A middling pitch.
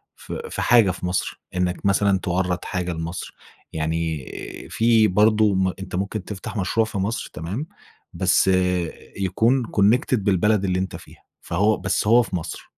No: very low, 95 Hz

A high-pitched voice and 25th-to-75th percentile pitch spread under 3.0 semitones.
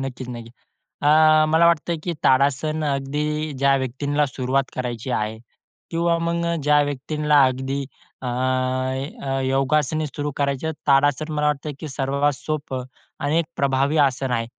No: medium, 140 Hz; narrow, 2.4 semitones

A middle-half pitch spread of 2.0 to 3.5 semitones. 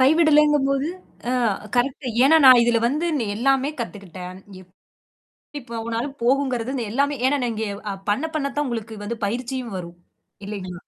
No: average, 3.9 semitones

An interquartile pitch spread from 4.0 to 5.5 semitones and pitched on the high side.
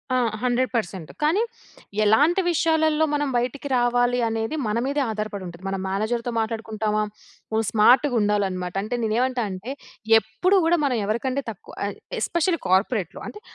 Yes: average, 4.7 semitones; high, 230 Hz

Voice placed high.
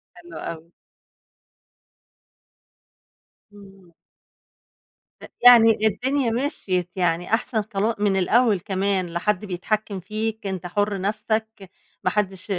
Yes: high, 200 Hz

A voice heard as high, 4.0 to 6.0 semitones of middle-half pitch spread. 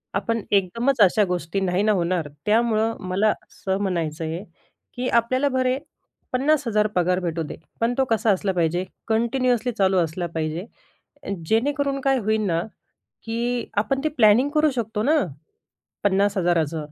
Yes: high, 215 Hz; average, 5.2 semitones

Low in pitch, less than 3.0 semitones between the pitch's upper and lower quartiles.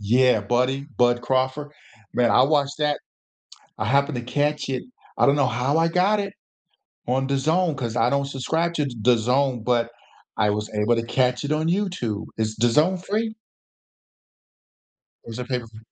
No: low, 130 Hz; average, 3.7 semitones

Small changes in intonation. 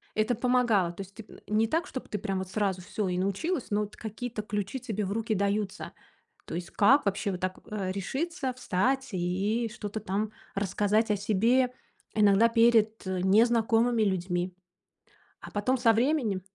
No: average, 3.3 semitones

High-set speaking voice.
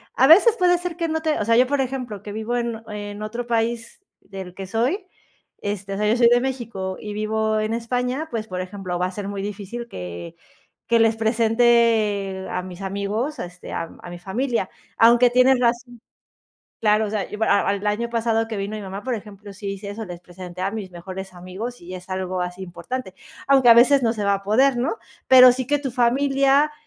Yes: high, 220 Hz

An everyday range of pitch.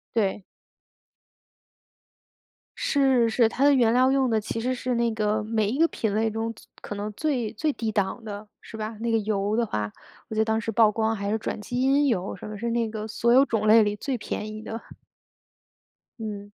No: narrow, 2.1 semitones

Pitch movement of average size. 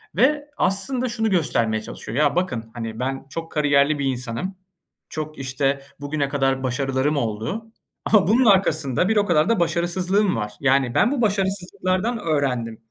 No: wide, 6.6 semitones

